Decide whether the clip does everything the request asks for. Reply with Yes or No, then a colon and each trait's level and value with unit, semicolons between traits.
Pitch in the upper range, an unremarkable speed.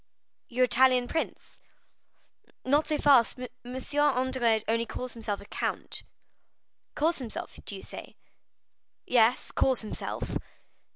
No: very high, 250 Hz; slow, 110 wpm